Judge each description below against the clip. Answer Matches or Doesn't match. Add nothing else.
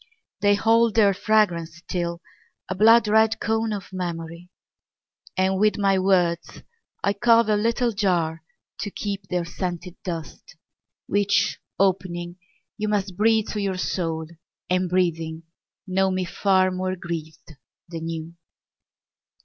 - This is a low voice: Doesn't match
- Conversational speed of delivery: Doesn't match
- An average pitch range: Matches